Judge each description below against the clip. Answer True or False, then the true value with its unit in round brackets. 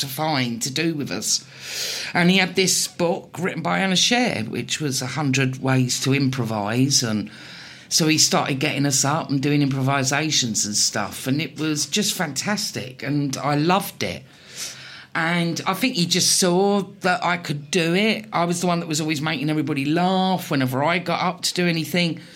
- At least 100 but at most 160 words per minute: False (190 wpm)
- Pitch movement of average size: True (4.4 semitones)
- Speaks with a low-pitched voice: False (155 Hz)